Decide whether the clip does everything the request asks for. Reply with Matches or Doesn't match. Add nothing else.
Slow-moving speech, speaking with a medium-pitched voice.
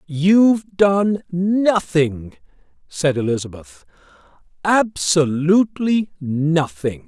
Matches